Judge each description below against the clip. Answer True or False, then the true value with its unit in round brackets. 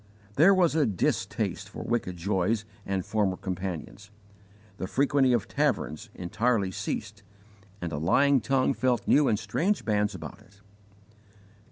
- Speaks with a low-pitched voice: True (105 Hz)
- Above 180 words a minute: False (140 wpm)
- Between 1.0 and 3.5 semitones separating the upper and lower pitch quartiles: False (5.5 semitones)